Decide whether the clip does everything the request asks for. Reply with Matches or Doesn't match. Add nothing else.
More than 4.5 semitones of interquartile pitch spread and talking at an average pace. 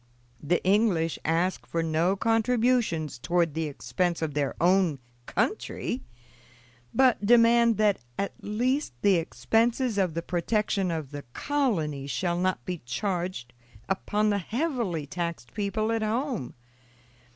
Doesn't match